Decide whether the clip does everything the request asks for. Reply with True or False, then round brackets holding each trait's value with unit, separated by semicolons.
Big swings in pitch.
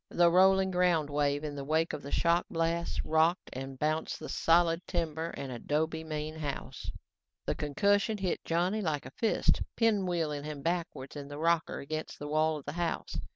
False (2.8 semitones)